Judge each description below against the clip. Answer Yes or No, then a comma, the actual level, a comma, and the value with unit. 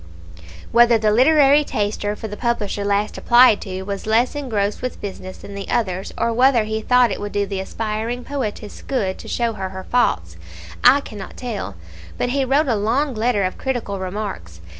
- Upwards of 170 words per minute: Yes, average, 185 wpm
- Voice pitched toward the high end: Yes, high, 215 Hz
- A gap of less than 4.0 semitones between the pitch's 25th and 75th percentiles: Yes, average, 3.6 semitones